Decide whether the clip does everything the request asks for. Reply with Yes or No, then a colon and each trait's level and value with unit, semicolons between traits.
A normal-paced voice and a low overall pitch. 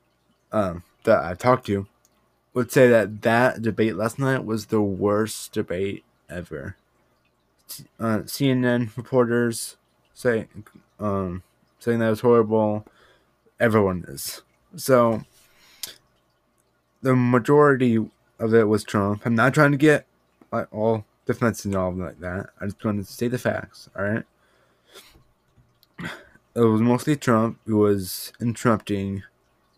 No: slow, 125 wpm; low, 110 Hz